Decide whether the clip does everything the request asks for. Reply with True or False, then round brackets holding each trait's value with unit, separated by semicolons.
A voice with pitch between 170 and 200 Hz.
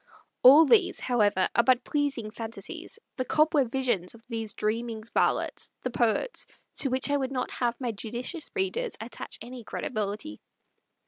False (245 Hz)